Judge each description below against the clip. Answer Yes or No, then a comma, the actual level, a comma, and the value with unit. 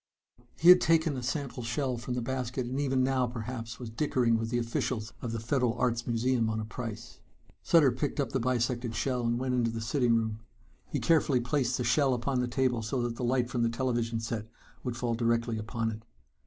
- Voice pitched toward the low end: Yes, low, 120 Hz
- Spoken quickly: Yes, fast, 215 wpm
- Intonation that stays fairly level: Yes, narrow, 2.1 semitones